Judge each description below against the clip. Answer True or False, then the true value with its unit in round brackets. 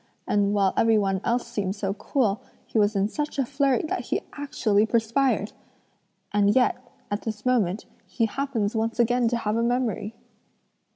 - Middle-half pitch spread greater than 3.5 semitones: False (3.2 semitones)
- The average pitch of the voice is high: True (225 Hz)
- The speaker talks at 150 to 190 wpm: True (170 wpm)